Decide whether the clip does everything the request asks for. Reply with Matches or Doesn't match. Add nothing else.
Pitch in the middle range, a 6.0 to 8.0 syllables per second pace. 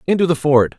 Matches